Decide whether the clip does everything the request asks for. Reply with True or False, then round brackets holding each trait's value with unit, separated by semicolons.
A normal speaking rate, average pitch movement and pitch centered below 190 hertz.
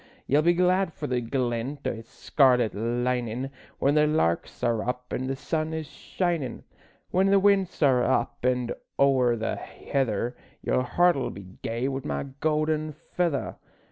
True (160 wpm; 4.3 semitones; 135 Hz)